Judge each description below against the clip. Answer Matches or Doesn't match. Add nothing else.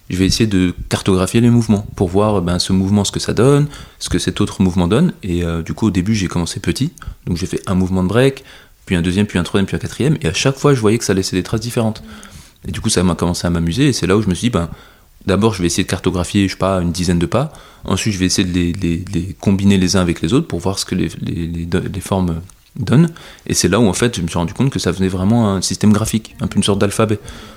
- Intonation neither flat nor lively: Matches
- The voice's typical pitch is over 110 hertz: Doesn't match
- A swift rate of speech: Matches